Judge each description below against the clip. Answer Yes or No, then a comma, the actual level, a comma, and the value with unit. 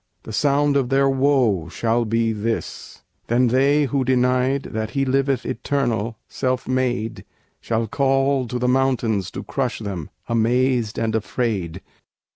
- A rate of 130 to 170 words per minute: Yes, average, 140 wpm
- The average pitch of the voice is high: No, low, 125 Hz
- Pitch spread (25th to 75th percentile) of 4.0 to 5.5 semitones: No, average, 3.2 semitones